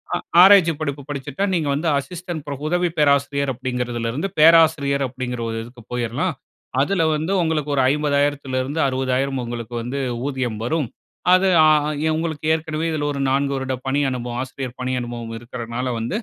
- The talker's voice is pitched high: No, medium, 140 Hz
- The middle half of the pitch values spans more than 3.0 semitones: Yes, average, 3.8 semitones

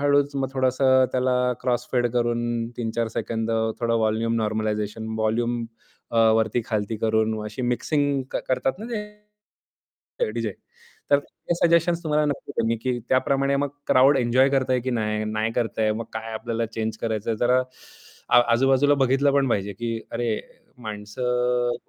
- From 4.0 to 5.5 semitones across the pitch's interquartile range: No, average, 3.0 semitones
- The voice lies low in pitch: Yes, low, 120 Hz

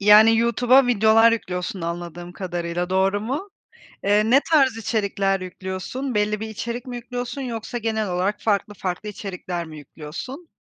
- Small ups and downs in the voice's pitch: No, average, 4.3 semitones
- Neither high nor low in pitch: No, high, 210 Hz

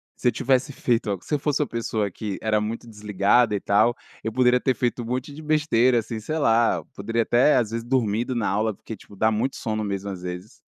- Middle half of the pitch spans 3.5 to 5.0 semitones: No, average, 3.1 semitones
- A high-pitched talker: No, low, 115 Hz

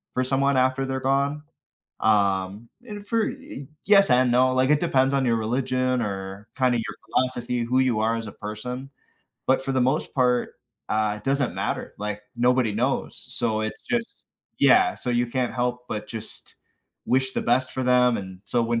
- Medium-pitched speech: No, low, 125 Hz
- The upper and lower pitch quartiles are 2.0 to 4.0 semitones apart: Yes, average, 2.7 semitones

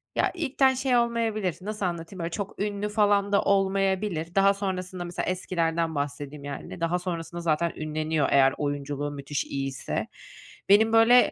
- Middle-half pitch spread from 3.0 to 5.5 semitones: Yes, average, 4.7 semitones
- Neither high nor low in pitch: Yes, medium, 180 Hz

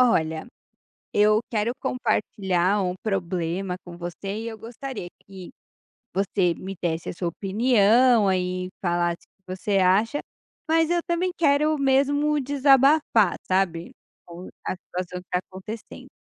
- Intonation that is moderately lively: No, wide, 5.8 semitones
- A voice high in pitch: Yes, high, 195 Hz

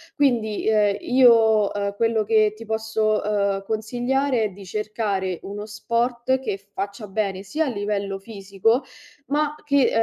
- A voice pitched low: No, high, 215 Hz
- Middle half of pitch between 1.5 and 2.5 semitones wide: No, average, 2.9 semitones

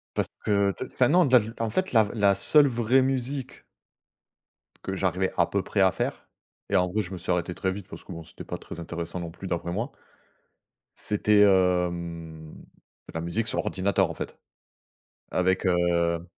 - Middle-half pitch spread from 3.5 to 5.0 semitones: Yes, average, 3.9 semitones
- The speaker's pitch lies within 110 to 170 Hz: No, very low, 95 Hz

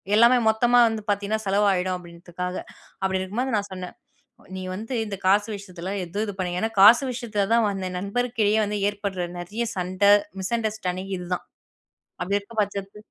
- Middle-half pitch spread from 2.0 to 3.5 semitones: Yes, average, 2.8 semitones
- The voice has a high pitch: Yes, high, 200 Hz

